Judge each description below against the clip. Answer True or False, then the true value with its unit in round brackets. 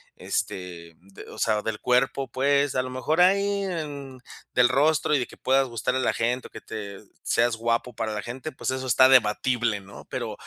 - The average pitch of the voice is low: True (125 Hz)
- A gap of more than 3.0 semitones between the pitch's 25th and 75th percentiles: True (3.4 semitones)